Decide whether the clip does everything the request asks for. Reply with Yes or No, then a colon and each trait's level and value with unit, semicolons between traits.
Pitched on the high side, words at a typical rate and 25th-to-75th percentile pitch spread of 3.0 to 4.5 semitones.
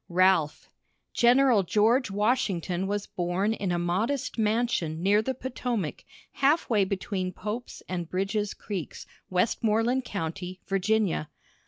No: high, 205 Hz; slow, 120 wpm; average, 3.9 semitones